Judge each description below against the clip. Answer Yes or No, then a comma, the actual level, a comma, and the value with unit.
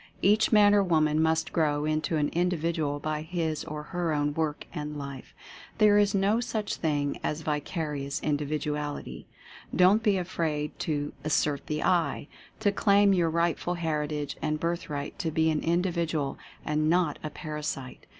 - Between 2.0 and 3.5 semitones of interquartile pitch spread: Yes, average, 2.9 semitones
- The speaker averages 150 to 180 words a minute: Yes, average, 165 wpm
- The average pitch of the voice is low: No, medium, 155 Hz